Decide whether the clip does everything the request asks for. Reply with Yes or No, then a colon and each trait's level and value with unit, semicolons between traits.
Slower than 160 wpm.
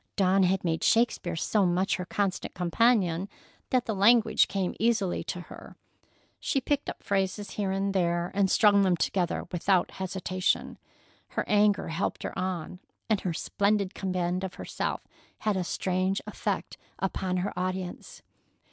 Yes: average, 150 wpm